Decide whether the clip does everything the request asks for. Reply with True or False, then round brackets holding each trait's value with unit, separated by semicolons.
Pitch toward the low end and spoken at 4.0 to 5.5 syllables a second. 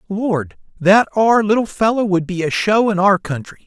False (200 Hz; 5.0 syllables/s)